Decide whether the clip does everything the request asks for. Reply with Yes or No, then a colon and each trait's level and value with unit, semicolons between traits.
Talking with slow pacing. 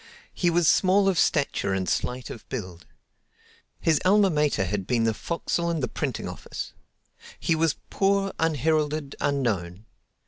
No: average, 145 wpm